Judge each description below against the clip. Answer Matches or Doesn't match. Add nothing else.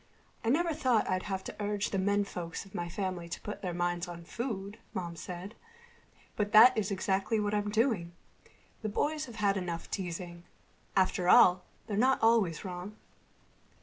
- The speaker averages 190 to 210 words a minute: Doesn't match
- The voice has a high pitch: Matches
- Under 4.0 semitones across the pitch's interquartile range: Matches